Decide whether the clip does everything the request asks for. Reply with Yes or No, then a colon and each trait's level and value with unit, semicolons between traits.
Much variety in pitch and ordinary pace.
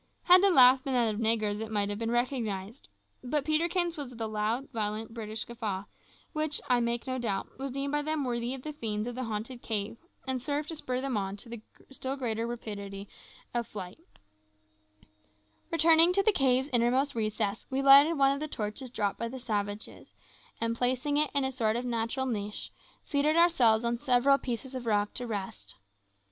No: average, 4.0 semitones; average, 195 wpm